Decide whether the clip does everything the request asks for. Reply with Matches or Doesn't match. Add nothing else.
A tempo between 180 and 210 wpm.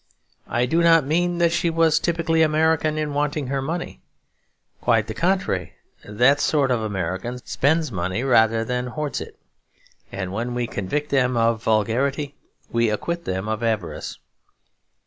Doesn't match